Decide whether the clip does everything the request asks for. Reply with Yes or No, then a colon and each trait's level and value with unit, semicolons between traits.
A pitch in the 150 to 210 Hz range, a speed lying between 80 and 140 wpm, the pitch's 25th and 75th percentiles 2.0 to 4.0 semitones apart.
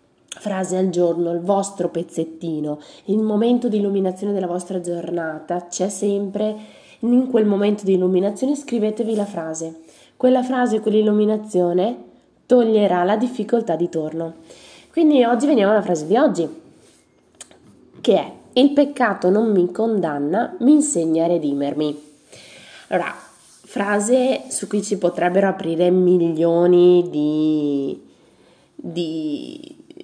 No: high, 190 Hz; average, 120 wpm; average, 4.5 semitones